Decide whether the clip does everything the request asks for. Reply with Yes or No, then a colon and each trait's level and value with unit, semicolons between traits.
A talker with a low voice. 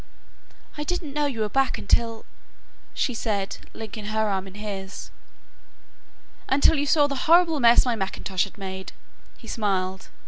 No: high, 220 Hz